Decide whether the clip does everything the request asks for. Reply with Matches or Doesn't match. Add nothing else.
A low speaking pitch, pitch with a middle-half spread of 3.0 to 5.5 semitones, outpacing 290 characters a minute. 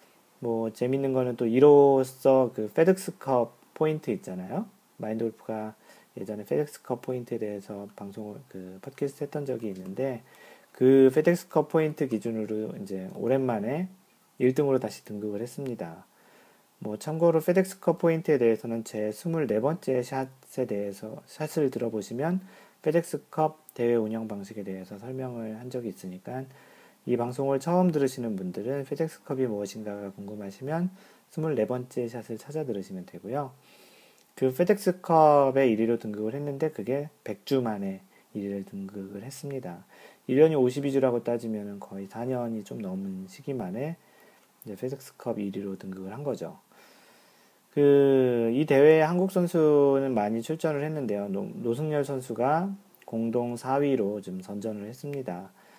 Doesn't match